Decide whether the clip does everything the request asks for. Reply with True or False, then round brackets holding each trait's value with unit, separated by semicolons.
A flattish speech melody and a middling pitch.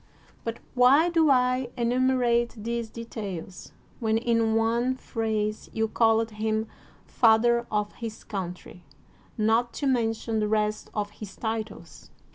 False (1.8 semitones; 225 Hz)